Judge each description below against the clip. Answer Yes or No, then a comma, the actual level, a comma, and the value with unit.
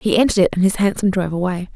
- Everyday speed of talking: No, fast, 275 wpm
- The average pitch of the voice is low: No, high, 190 Hz